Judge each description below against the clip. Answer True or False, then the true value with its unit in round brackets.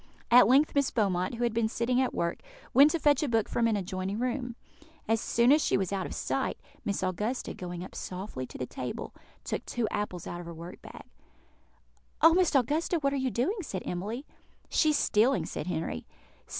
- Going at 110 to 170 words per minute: False (205 wpm)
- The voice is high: True (230 Hz)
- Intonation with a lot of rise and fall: True (6.2 semitones)